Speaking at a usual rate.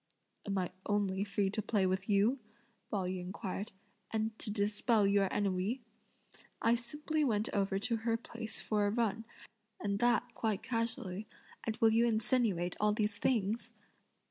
Yes: average, 155 wpm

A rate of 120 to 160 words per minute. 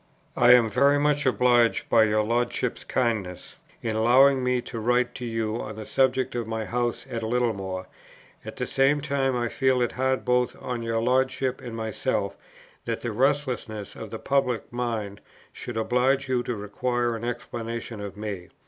No: average, 175 wpm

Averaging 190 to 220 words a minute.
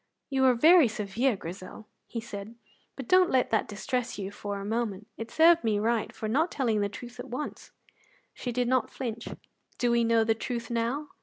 Yes: average, 200 wpm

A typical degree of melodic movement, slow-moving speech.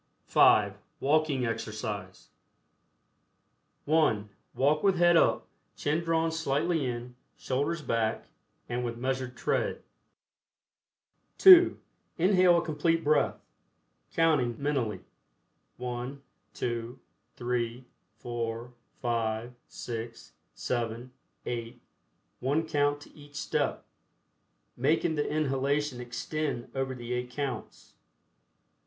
Yes: average, 4.3 semitones; slow, 95 wpm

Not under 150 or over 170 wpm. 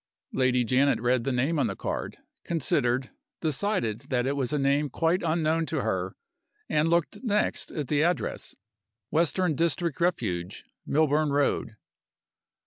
No: average, 140 wpm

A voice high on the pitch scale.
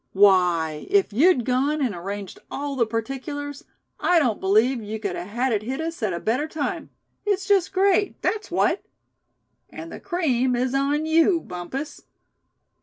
Yes: very high, 260 Hz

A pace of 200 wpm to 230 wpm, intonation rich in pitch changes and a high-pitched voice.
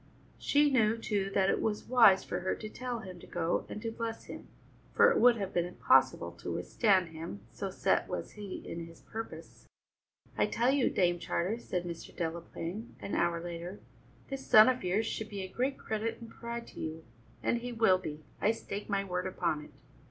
No: fast, 205 wpm; average, 4.6 semitones; high, 200 Hz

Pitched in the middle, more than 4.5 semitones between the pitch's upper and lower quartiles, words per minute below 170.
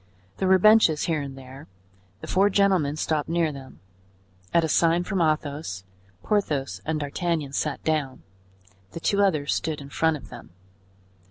No: medium, 155 Hz; average, 3.5 semitones; average, 160 wpm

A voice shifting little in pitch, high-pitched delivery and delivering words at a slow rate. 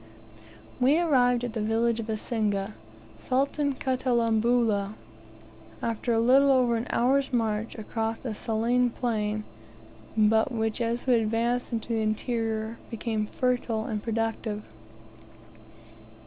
Yes: narrow, 2.1 semitones; high, 230 Hz; slow, 120 wpm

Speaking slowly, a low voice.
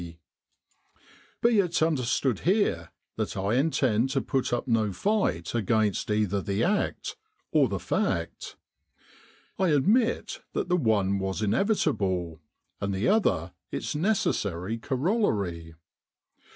Yes: slow, 125 wpm; low, 115 Hz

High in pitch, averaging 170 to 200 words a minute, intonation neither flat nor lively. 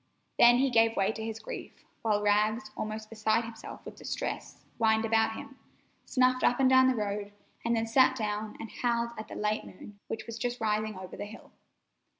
No: high, 225 Hz; average, 195 wpm; narrow, 1.8 semitones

